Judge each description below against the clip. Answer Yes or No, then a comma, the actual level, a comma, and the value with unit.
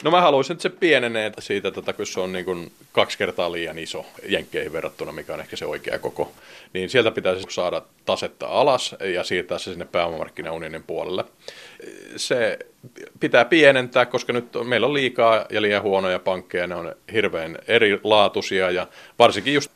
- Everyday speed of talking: No, fast, 170 wpm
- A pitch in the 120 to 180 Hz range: Yes, medium, 140 Hz